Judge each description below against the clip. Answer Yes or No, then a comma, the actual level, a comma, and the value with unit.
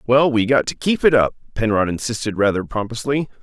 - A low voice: Yes, low, 120 Hz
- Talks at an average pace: Yes, average, 195 wpm